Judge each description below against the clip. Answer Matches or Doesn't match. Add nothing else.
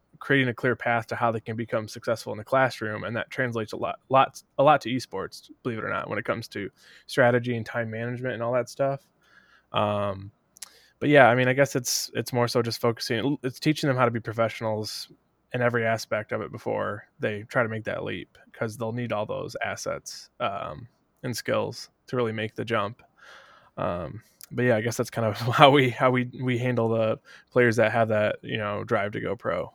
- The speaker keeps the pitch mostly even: Matches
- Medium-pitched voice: Doesn't match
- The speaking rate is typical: Doesn't match